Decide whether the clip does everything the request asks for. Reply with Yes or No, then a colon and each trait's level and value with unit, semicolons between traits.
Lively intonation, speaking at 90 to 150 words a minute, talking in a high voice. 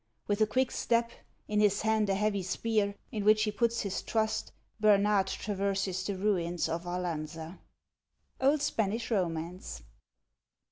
No: average, 3.0 semitones; average, 145 wpm; high, 205 Hz